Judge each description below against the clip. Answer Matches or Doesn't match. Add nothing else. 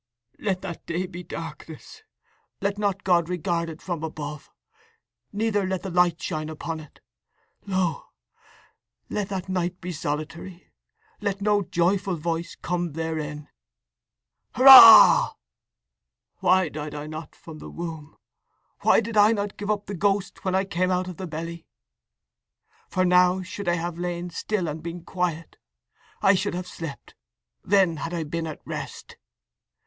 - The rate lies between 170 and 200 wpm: Doesn't match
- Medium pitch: Matches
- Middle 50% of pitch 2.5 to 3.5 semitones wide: Matches